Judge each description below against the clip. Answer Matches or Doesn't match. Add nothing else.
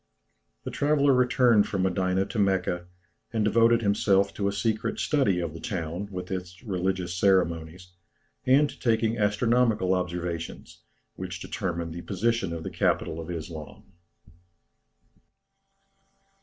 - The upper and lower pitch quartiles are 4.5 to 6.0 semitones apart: Doesn't match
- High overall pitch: Doesn't match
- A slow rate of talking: Matches